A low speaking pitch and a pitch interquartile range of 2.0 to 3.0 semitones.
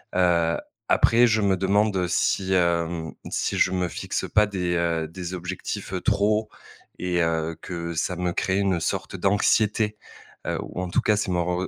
Yes: very low, 90 Hz; narrow, 2.6 semitones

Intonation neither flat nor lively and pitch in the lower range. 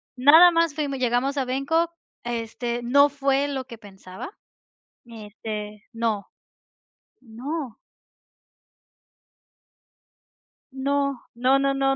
No: average, 3.4 semitones; very high, 265 Hz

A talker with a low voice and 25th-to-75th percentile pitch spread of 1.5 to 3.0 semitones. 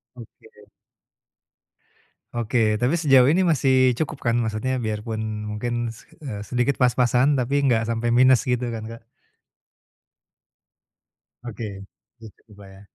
Yes: low, 120 Hz; narrow, 2.5 semitones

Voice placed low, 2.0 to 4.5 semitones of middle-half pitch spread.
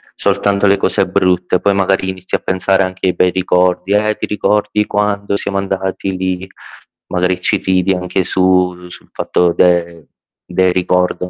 No: very low, 95 Hz; narrow, 1.3 semitones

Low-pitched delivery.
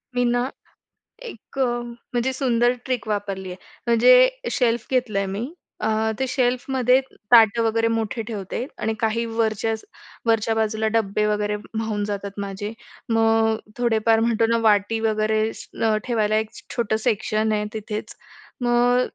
No: high, 225 Hz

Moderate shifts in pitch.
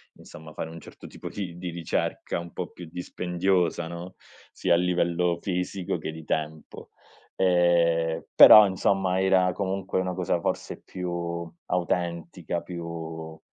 No: narrow, 1.7 semitones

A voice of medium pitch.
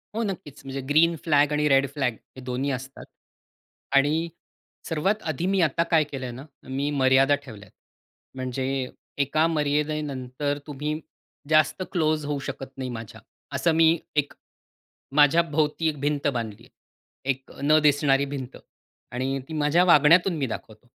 Yes: medium, 145 Hz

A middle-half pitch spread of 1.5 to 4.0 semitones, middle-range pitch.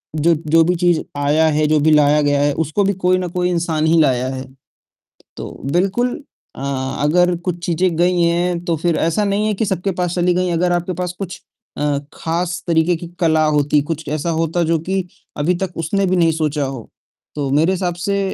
Yes: average, 2.7 semitones; medium, 170 Hz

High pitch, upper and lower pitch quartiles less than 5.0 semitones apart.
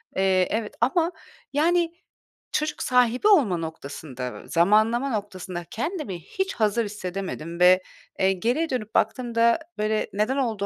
No: high, 215 Hz; wide, 5.5 semitones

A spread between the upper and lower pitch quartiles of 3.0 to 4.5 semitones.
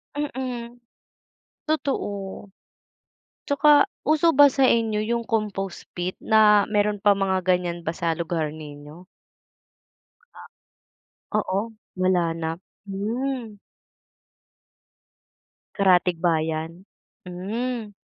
No: average, 4.9 semitones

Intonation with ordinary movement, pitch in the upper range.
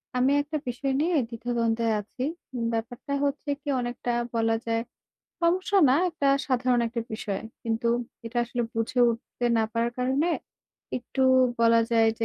Yes: average, 3.0 semitones; high, 240 Hz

